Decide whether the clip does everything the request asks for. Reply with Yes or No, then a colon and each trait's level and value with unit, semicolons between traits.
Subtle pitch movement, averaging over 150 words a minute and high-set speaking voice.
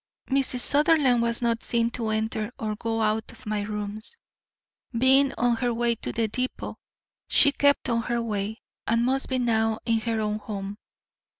Yes: narrow, 2.3 semitones; average, 175 wpm; high, 230 Hz